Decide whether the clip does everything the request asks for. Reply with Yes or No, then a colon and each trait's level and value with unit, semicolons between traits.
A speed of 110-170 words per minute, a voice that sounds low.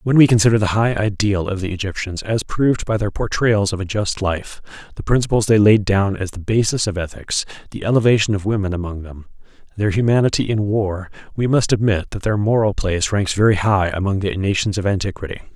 No: fast, 205 wpm; low, 105 Hz